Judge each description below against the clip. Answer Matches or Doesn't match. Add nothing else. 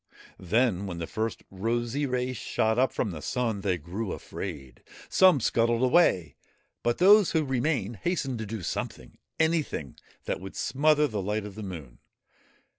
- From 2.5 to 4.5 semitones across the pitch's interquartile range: Doesn't match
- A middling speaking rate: Matches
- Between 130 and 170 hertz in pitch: Doesn't match